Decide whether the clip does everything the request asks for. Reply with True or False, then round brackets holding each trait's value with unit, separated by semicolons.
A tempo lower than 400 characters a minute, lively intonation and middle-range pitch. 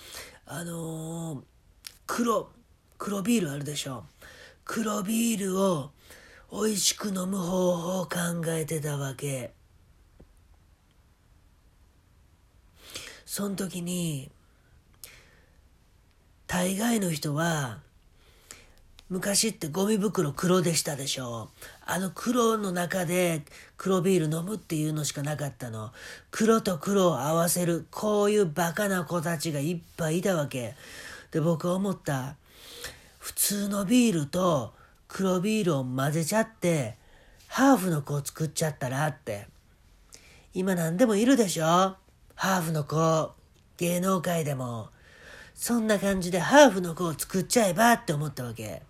True (235 characters per minute; 6.2 semitones; 165 Hz)